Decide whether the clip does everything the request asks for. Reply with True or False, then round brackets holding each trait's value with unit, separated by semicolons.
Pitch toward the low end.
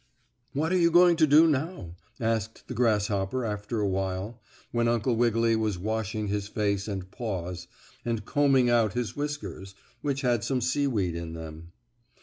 True (110 Hz)